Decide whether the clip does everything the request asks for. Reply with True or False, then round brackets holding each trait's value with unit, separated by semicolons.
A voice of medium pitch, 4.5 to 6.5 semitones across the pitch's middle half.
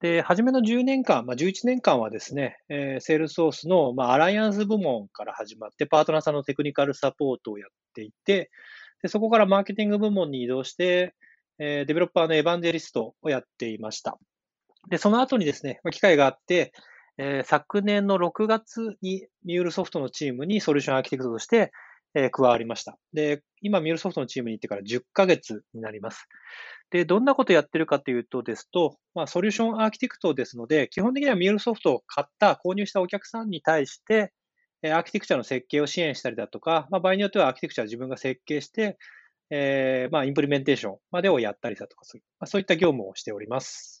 False (165 Hz; 6.9 semitones)